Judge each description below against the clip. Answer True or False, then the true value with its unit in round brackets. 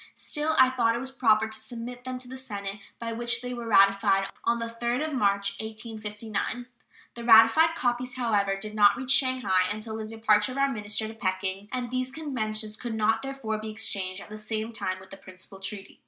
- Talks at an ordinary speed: False (210 wpm)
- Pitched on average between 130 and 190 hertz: False (225 Hz)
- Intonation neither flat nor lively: True (3.0 semitones)